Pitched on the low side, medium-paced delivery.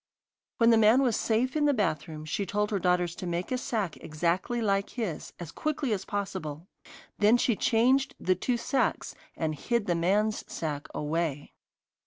No: high, 200 Hz; average, 175 wpm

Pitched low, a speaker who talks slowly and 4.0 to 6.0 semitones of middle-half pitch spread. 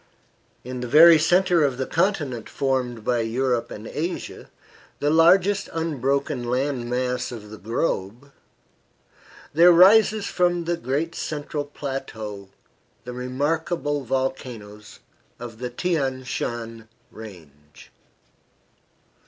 Yes: low, 130 Hz; slow, 110 wpm; wide, 5.5 semitones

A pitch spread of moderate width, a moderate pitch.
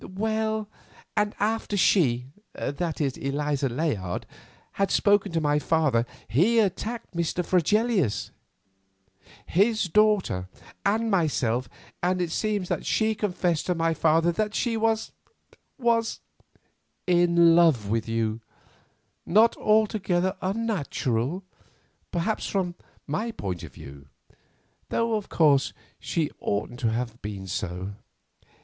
No: wide, 7.8 semitones; medium, 175 Hz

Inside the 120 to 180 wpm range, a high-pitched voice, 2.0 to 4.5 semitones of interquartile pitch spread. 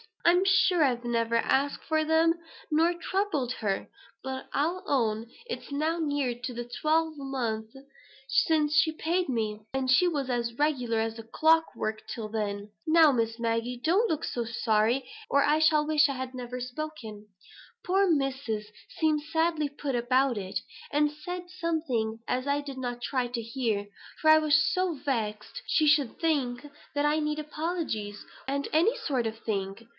No: average, 160 wpm; very high, 275 Hz; average, 5.0 semitones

